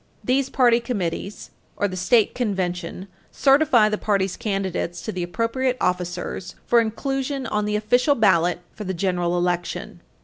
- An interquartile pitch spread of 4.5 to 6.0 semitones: Yes, average, 5.1 semitones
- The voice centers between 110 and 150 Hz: No, high, 210 Hz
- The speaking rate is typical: Yes, average, 145 wpm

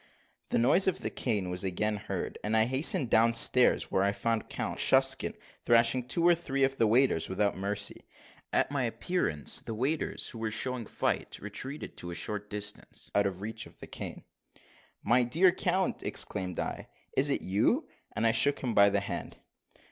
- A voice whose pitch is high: No, low, 115 Hz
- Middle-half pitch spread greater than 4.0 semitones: Yes, average, 4.9 semitones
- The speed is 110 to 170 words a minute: No, average, 185 wpm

